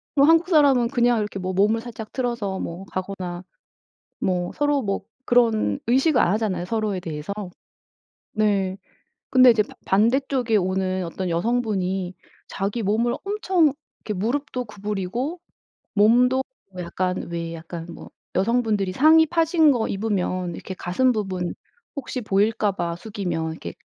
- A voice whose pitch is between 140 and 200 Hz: No, high, 210 Hz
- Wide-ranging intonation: No, average, 5.0 semitones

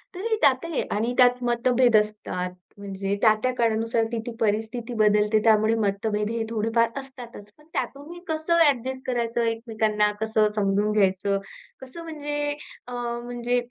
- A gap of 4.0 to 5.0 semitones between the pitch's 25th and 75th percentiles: No, average, 3.2 semitones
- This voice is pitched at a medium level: No, high, 230 Hz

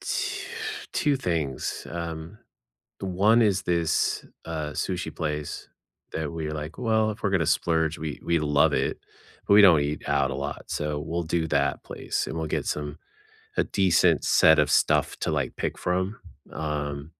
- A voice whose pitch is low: Yes, very low, 80 Hz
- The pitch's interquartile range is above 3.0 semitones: Yes, average, 3.6 semitones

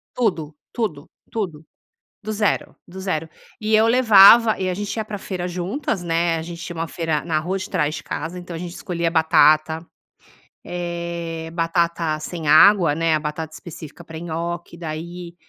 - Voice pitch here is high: No, medium, 170 Hz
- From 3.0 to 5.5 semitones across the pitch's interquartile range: No, narrow, 2.5 semitones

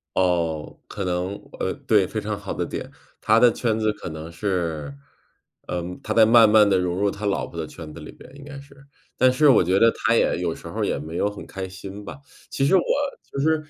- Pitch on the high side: No, low, 100 Hz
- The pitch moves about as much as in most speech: Yes, average, 4.1 semitones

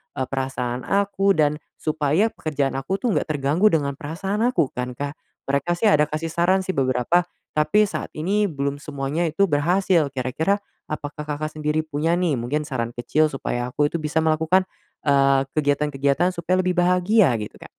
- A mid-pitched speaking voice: Yes, medium, 155 Hz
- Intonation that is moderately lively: Yes, average, 4.1 semitones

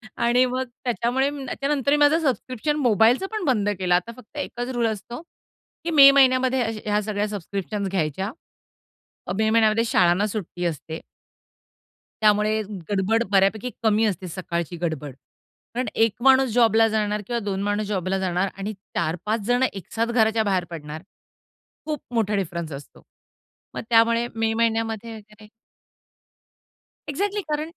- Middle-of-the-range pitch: No, high, 220 Hz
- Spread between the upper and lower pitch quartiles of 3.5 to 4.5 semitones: Yes, average, 3.9 semitones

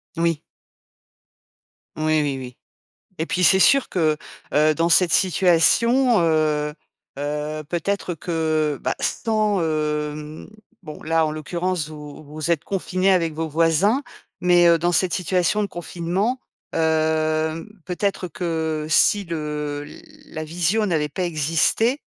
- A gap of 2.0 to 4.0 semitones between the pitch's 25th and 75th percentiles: Yes, average, 2.9 semitones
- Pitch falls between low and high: Yes, medium, 165 Hz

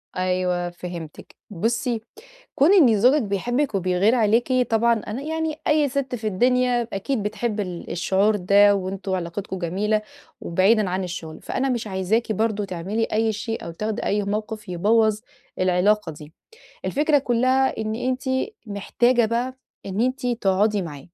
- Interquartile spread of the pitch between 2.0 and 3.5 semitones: No, average, 4.3 semitones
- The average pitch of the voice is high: Yes, high, 215 Hz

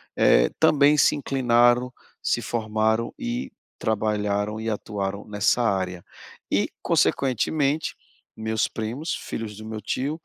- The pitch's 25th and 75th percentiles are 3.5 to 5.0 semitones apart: Yes, average, 3.9 semitones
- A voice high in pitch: No, low, 110 Hz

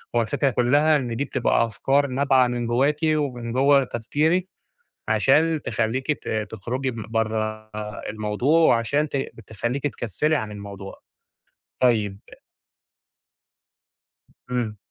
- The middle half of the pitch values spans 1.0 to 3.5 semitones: No, average, 4.2 semitones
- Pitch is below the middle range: Yes, low, 125 Hz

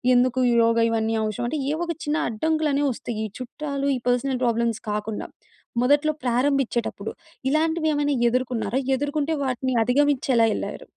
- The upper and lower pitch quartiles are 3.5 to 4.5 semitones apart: Yes, average, 3.8 semitones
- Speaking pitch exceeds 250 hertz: Yes, very high, 260 Hz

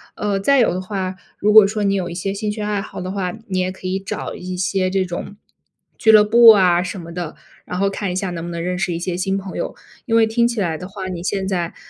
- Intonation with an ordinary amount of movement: No, narrow, 2.2 semitones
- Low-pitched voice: No, high, 190 Hz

